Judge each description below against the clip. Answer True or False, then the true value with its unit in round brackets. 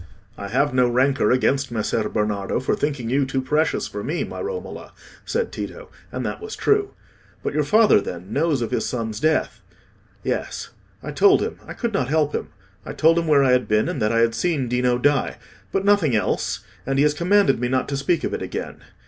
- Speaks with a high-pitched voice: False (135 Hz)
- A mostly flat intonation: False (5.1 semitones)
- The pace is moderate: False (210 wpm)